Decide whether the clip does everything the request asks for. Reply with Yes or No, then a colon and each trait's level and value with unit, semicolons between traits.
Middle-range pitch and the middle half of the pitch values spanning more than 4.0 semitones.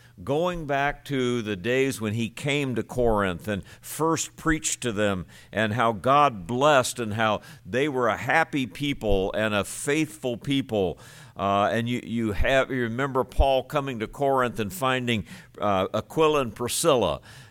No: low, 120 Hz; average, 4.4 semitones